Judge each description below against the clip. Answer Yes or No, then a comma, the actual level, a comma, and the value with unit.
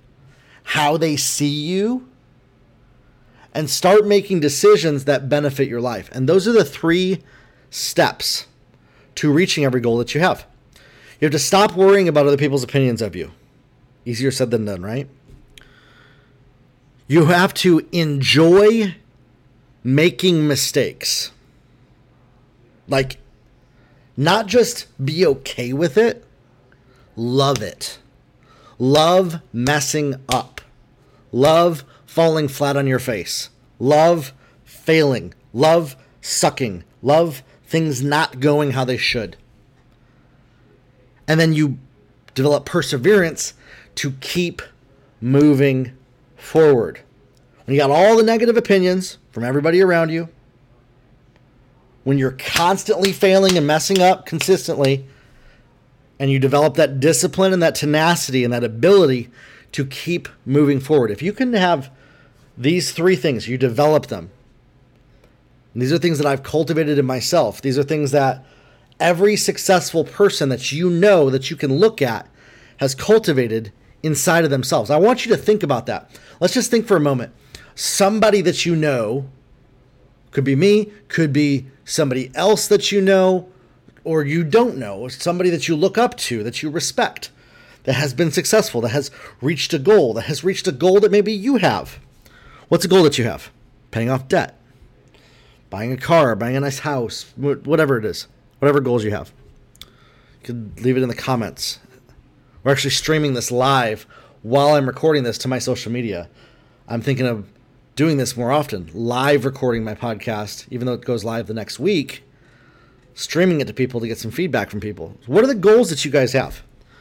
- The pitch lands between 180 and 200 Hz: No, medium, 140 Hz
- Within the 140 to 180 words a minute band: Yes, average, 150 wpm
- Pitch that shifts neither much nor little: Yes, average, 4.5 semitones